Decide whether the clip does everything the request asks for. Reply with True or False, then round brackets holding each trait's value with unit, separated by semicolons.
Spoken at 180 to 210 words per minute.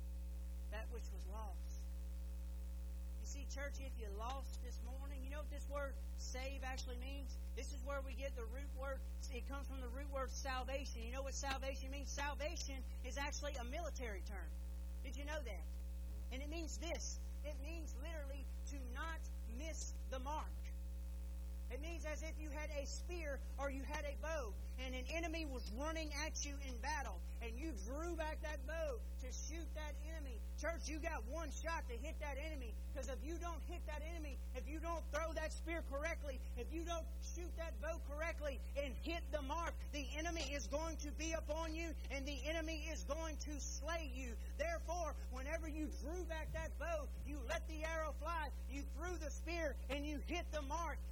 True (195 wpm)